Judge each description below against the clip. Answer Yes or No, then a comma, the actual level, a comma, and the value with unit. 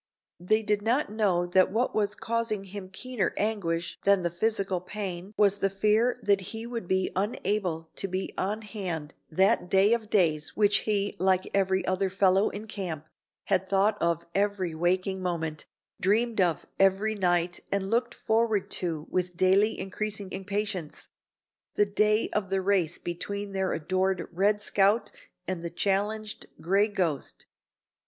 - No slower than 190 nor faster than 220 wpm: No, average, 155 wpm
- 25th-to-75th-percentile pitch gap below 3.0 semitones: Yes, narrow, 2.5 semitones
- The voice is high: Yes, high, 195 Hz